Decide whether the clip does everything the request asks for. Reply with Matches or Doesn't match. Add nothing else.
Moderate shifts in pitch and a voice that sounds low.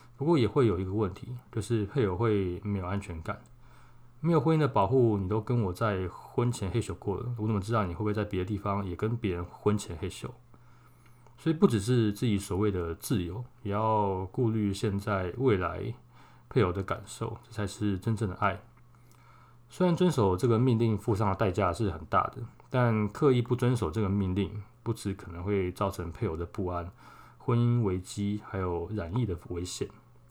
Matches